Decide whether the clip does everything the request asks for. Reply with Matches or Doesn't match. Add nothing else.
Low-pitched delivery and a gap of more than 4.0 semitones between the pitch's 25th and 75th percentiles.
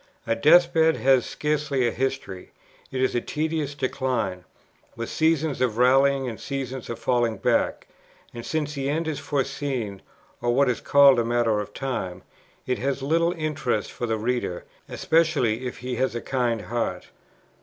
Doesn't match